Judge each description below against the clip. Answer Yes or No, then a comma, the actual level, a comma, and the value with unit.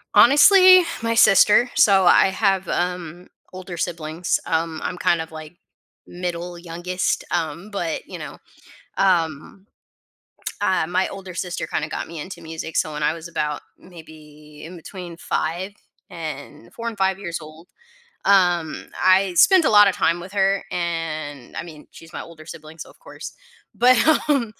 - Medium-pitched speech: Yes, medium, 175 Hz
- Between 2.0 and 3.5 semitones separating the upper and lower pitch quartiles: Yes, average, 3.2 semitones